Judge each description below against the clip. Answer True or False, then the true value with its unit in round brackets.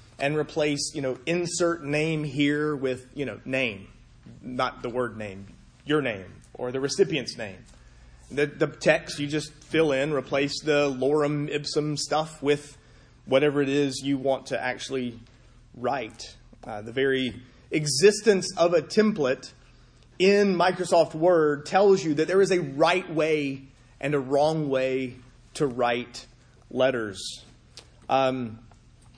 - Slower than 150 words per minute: True (140 wpm)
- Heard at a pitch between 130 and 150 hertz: True (140 Hz)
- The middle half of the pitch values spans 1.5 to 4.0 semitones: True (3.7 semitones)